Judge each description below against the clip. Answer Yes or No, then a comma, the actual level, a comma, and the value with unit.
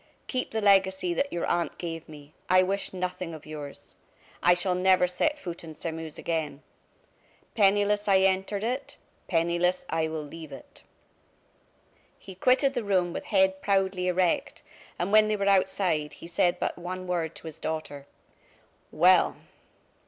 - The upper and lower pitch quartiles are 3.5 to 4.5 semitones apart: No, average, 3.0 semitones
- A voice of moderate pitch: Yes, medium, 180 Hz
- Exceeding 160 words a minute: No, average, 155 wpm